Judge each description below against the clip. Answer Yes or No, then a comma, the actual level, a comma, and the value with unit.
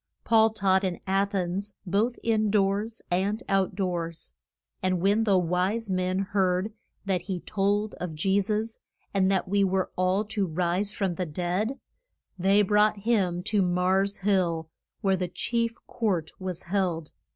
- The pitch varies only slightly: Yes, narrow, 2.3 semitones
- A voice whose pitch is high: Yes, high, 195 Hz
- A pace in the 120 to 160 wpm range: Yes, average, 155 wpm